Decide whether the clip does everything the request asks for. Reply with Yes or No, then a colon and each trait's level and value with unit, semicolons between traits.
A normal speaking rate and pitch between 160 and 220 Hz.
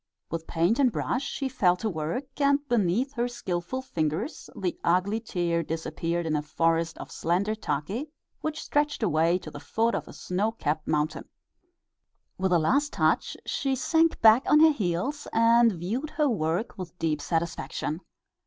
Yes: average, 165 wpm; high, 190 Hz